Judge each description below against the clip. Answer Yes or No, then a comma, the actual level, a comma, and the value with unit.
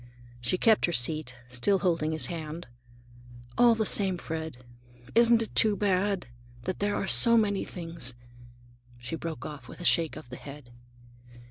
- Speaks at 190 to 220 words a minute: No, average, 160 wpm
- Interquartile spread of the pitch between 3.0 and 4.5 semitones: No, wide, 5.5 semitones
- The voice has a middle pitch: Yes, medium, 170 Hz